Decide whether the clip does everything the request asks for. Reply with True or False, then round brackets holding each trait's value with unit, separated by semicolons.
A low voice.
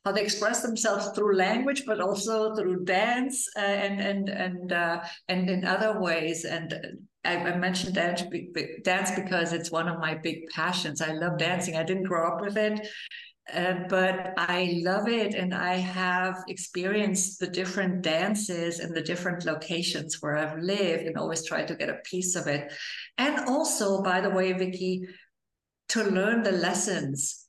False (185 Hz)